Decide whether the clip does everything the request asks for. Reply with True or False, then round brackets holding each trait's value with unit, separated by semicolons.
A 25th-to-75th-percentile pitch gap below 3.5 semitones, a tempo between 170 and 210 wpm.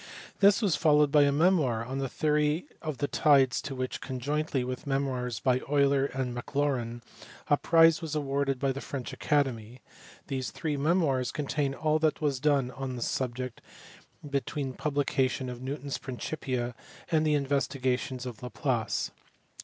False (2.6 semitones; 160 wpm)